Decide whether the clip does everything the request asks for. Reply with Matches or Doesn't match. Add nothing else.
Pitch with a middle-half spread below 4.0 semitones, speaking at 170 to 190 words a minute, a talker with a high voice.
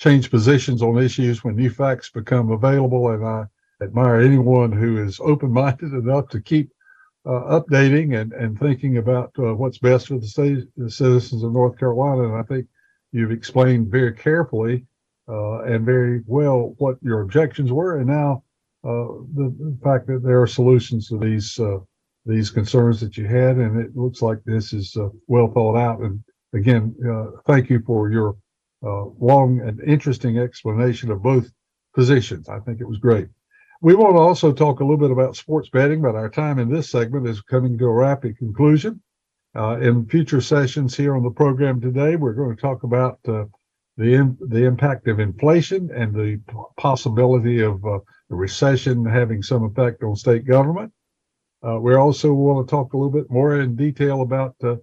Doesn't match